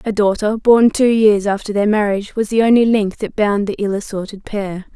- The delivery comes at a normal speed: No, fast, 220 wpm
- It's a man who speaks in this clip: No, female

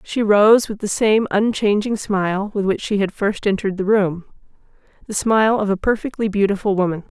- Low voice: No, high, 205 Hz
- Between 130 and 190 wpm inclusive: Yes, average, 175 wpm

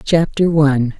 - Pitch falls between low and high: Yes, medium, 150 Hz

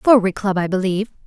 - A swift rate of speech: No, average, 190 wpm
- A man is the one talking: No, female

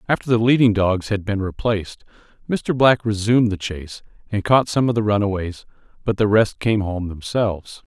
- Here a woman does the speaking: No, male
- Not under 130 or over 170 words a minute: No, average, 180 wpm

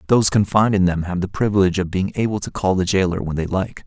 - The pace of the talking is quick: Yes, fast, 265 wpm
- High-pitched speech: No, very low, 95 Hz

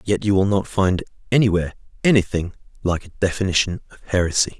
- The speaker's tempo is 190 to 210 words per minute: No, average, 155 wpm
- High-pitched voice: No, very low, 95 Hz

